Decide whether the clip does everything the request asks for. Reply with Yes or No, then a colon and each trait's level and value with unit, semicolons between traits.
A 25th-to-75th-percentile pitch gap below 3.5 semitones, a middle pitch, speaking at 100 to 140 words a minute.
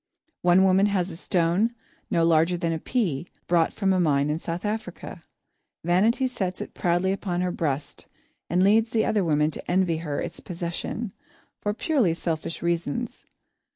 No: average, 2.9 semitones; medium, 175 Hz; average, 160 wpm